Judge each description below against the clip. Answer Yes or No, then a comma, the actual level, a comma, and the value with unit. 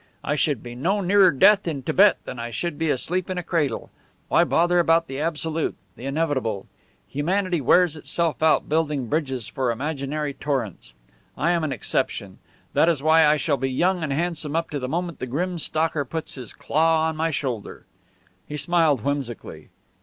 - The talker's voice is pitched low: No, medium, 155 Hz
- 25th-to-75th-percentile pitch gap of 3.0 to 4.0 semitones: Yes, average, 3.6 semitones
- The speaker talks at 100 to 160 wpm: No, average, 185 wpm